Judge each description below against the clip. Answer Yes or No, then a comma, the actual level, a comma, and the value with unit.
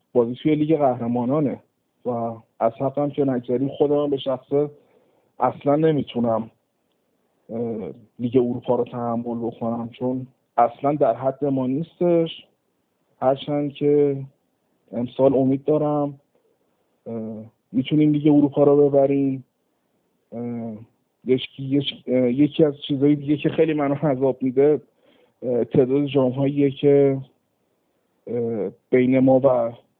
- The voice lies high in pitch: No, low, 135 Hz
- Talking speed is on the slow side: Yes, slow, 100 wpm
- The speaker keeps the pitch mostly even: No, average, 3.0 semitones